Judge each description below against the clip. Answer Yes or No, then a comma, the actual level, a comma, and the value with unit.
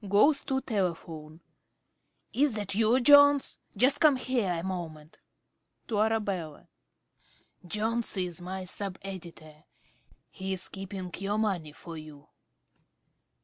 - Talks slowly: Yes, slow, 115 wpm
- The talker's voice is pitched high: Yes, high, 195 Hz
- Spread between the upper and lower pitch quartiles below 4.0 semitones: No, average, 4.6 semitones